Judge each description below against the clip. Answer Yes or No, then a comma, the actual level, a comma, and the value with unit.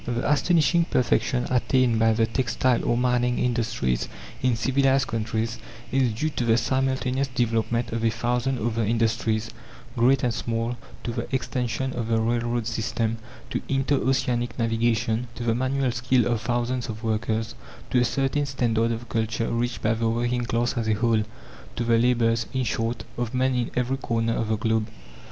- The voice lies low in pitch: Yes, low, 120 Hz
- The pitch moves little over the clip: Yes, narrow, 1.8 semitones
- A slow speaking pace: No, average, 175 wpm